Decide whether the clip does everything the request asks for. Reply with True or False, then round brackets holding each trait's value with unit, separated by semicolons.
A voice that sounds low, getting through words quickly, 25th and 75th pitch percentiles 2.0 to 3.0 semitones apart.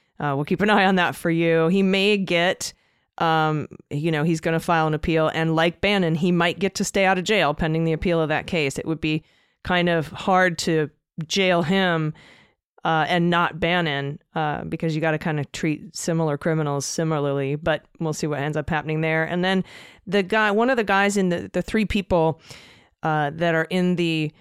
False (165 Hz; 215 wpm; 2.7 semitones)